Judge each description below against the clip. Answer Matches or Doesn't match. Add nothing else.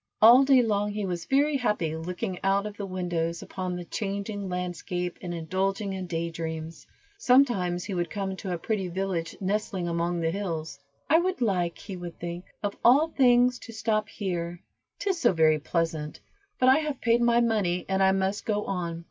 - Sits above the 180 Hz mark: Matches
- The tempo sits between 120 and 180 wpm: Doesn't match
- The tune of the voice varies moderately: Matches